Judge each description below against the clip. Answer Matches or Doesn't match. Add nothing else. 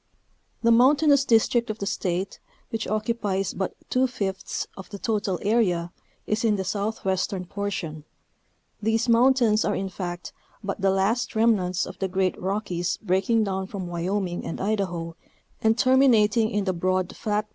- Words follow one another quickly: Doesn't match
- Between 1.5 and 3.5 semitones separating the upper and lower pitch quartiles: Matches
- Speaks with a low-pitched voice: Doesn't match